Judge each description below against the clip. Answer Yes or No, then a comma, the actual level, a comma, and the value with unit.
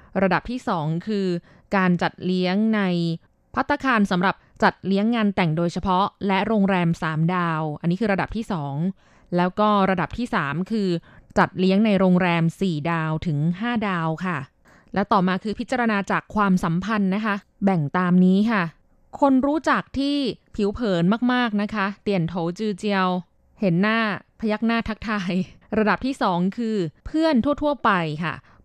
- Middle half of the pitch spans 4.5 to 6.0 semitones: No, average, 3.7 semitones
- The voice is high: Yes, high, 195 Hz